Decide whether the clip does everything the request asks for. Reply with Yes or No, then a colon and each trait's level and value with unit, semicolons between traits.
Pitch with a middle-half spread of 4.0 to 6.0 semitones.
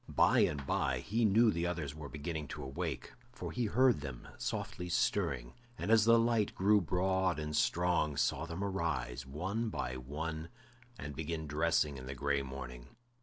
Yes: average, 5.2 semitones